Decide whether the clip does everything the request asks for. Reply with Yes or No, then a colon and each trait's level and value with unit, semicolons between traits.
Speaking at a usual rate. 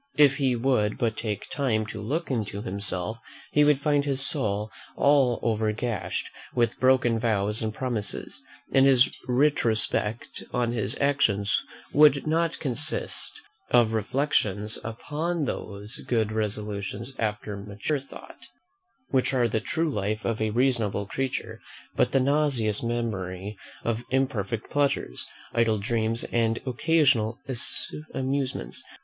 No: slow, 130 wpm